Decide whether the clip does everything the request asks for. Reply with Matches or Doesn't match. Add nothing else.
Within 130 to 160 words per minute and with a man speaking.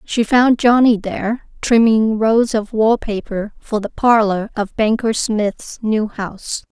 Doesn't match